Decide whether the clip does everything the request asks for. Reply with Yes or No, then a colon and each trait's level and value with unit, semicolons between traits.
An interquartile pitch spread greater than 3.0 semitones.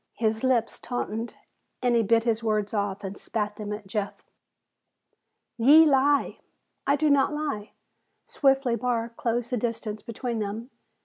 Yes: average, 3.4 semitones